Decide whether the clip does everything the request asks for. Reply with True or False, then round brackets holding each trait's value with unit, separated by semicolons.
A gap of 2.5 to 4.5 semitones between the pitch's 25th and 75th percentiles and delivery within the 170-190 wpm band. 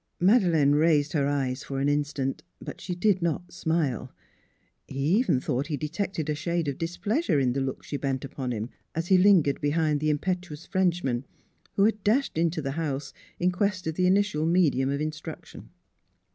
True (4.1 semitones; 185 wpm)